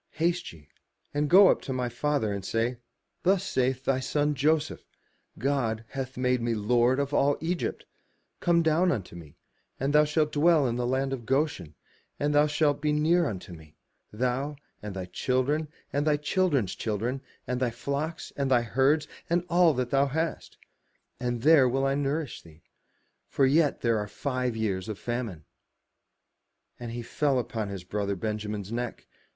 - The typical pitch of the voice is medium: No, low, 130 Hz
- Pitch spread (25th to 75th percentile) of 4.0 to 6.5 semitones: Yes, average, 4.4 semitones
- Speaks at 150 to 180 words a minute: Yes, average, 170 wpm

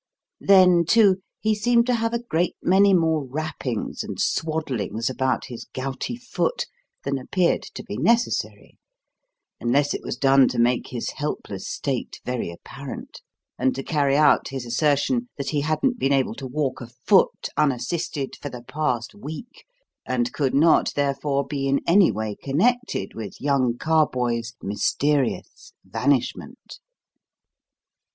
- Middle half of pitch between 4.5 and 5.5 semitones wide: Yes, average, 5.0 semitones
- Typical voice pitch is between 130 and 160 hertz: Yes, medium, 140 Hz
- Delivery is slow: No, average, 145 wpm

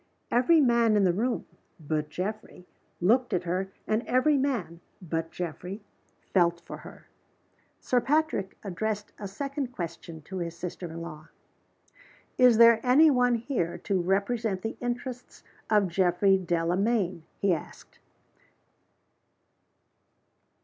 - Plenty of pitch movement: Yes, wide, 5.7 semitones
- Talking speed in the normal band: No, slow, 130 wpm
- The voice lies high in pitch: Yes, high, 200 Hz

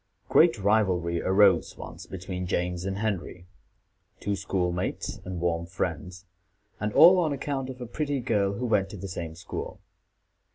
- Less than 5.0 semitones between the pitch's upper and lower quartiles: Yes, average, 3.7 semitones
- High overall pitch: No, very low, 95 Hz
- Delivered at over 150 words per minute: Yes, average, 160 wpm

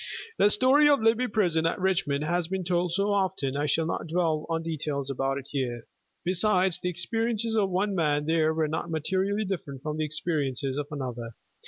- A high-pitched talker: No, medium, 165 Hz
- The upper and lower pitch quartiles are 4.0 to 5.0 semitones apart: Yes, average, 4.6 semitones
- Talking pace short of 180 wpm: No, average, 190 wpm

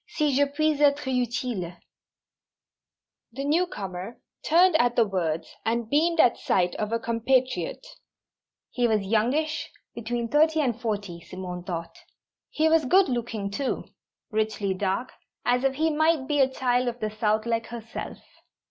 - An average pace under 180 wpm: Yes, average, 150 wpm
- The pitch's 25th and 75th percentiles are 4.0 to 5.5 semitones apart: Yes, average, 5.2 semitones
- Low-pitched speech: No, high, 240 Hz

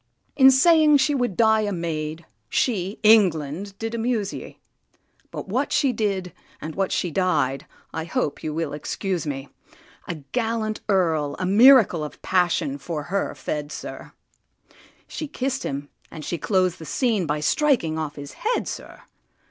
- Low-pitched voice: No, medium, 185 Hz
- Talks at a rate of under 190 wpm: Yes, average, 155 wpm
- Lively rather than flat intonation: Yes, wide, 6.5 semitones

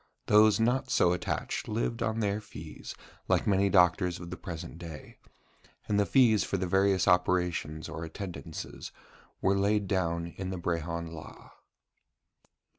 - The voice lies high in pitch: No, very low, 95 Hz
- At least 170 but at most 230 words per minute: No, average, 145 wpm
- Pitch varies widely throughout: No, average, 3.3 semitones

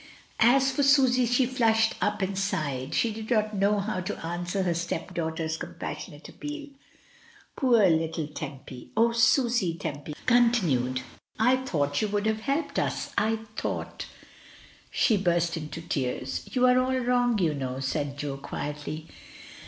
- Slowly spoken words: No, average, 155 wpm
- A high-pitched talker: Yes, high, 195 Hz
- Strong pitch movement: Yes, wide, 7.4 semitones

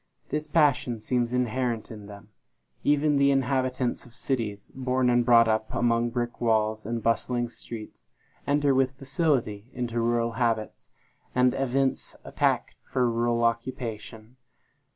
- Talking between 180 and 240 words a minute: No, slow, 135 wpm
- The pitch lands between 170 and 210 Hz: No, low, 120 Hz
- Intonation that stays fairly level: Yes, narrow, 2.2 semitones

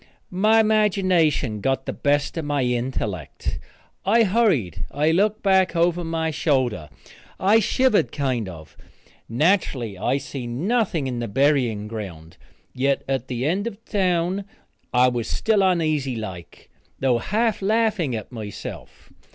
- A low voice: No, medium, 145 Hz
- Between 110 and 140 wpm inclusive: Yes, slow, 135 wpm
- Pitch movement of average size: No, wide, 8.1 semitones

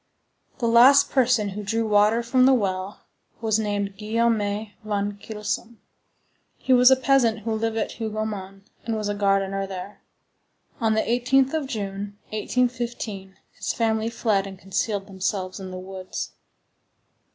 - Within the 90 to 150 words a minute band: Yes, average, 140 wpm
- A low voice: No, high, 215 Hz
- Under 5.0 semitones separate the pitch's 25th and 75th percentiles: Yes, average, 2.8 semitones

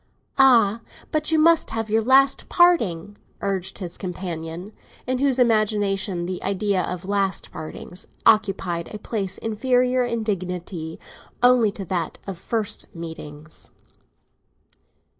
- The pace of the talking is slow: Yes, slow, 120 wpm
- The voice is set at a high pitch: Yes, high, 205 Hz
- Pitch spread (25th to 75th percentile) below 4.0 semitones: No, average, 4.5 semitones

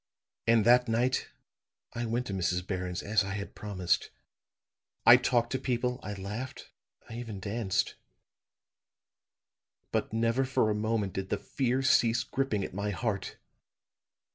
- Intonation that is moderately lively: Yes, average, 3.6 semitones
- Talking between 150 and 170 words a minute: No, average, 140 wpm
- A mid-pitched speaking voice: No, low, 110 Hz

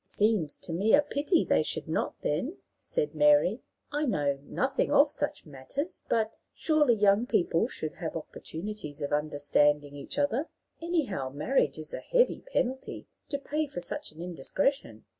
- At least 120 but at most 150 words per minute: No, average, 160 wpm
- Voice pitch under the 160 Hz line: No, high, 200 Hz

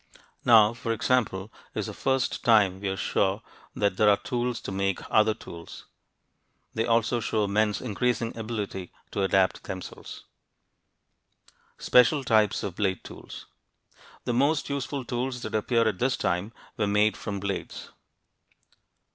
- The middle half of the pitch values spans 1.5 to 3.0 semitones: No, average, 3.5 semitones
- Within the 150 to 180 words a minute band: No, average, 140 wpm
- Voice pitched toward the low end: Yes, low, 110 Hz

